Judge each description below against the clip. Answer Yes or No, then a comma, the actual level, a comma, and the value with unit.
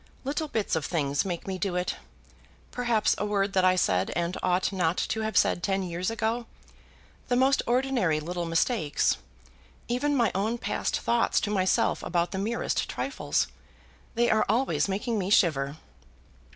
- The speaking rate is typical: Yes, average, 165 wpm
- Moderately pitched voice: No, high, 195 Hz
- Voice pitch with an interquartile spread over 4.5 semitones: Yes, average, 4.9 semitones